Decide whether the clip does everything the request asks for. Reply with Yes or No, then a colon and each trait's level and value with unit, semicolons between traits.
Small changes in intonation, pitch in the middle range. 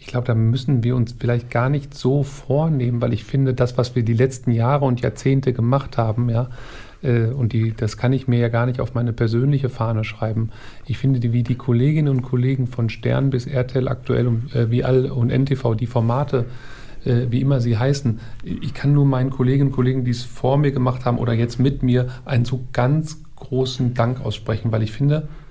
No: narrow, 2.1 semitones; low, 125 Hz